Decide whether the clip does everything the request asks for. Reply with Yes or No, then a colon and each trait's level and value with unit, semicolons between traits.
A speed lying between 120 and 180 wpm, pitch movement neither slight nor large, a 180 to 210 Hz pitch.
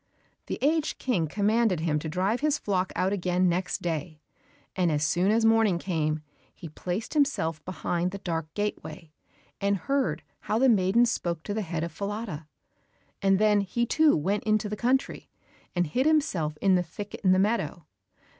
Yes: average, 175 wpm; average, 4.6 semitones; high, 190 Hz